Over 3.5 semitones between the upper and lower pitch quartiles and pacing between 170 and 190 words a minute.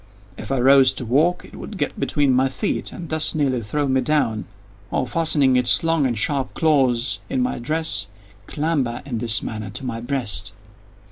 Yes: average, 4.2 semitones; average, 185 wpm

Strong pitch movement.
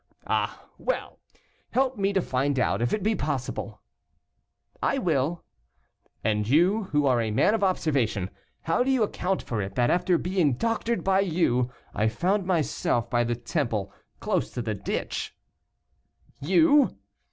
Yes: wide, 8.6 semitones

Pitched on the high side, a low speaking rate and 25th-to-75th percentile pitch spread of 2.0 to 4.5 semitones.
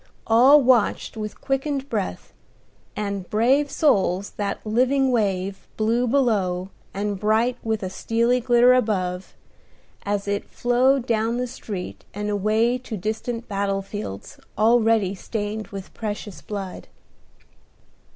Yes: high, 220 Hz; slow, 120 wpm; average, 3.3 semitones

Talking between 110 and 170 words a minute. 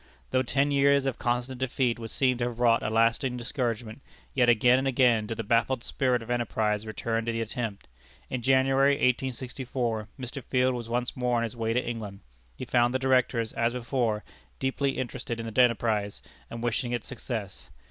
No: average, 190 wpm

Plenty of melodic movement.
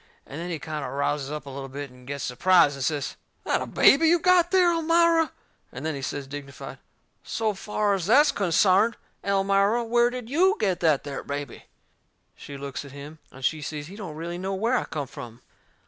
Yes: wide, 8.1 semitones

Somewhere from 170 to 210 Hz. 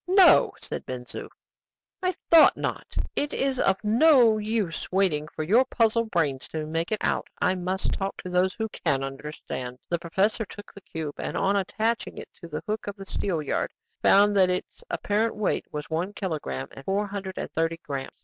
Yes: high, 190 Hz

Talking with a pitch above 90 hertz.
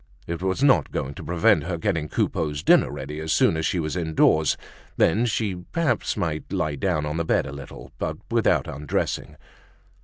No: very low, 80 Hz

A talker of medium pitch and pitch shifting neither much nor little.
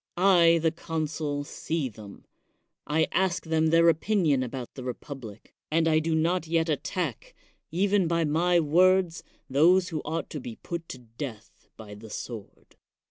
Yes: medium, 160 Hz; average, 3.8 semitones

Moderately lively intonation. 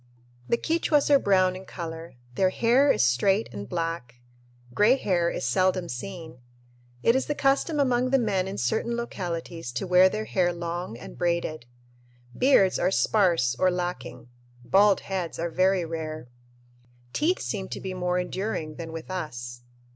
Yes: average, 4.0 semitones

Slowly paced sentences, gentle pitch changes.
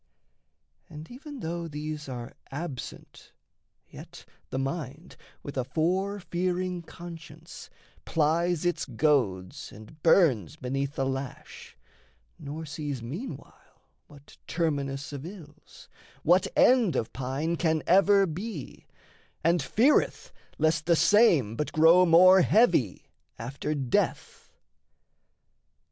No: slow, 110 wpm; average, 4.2 semitones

